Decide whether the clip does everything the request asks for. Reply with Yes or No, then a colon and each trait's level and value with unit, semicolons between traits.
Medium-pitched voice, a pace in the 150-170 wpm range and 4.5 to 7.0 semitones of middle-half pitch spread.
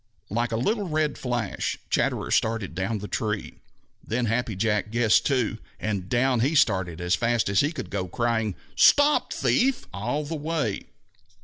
No: low, 115 Hz; average, 165 wpm; average, 5.2 semitones